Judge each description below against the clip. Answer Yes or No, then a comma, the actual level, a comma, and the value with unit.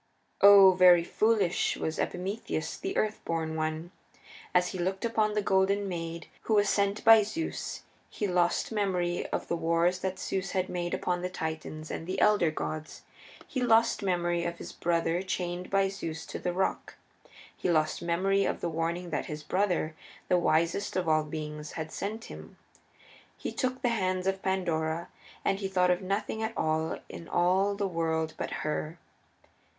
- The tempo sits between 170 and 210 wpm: Yes, average, 175 wpm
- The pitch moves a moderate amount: Yes, average, 3.0 semitones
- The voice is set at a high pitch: No, medium, 180 Hz